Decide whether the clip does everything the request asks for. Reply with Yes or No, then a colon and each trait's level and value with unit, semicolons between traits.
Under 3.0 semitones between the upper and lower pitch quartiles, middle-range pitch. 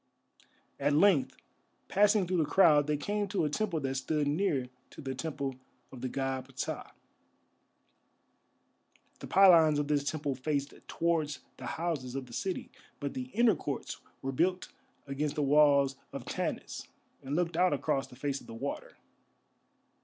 No: average, 3.9 semitones; medium, 145 Hz